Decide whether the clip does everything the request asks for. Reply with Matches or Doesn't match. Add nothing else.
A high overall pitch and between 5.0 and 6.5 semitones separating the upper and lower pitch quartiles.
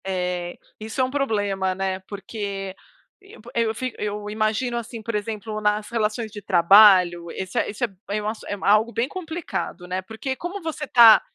Doesn't match